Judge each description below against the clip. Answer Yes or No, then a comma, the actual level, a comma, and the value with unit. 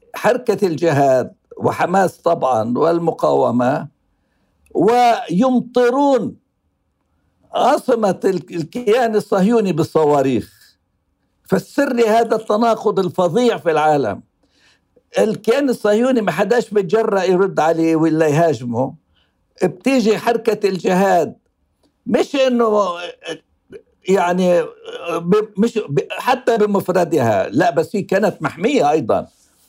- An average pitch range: No, wide, 6.0 semitones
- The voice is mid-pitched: No, high, 200 Hz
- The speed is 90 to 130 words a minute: No, average, 80 wpm